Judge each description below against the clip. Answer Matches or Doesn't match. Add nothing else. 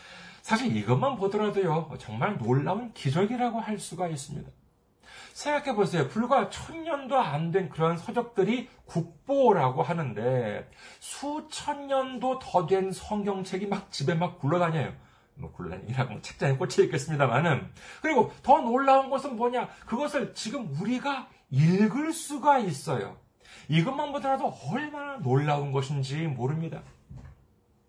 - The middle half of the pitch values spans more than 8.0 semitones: Matches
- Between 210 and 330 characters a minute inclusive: Matches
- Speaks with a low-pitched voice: Doesn't match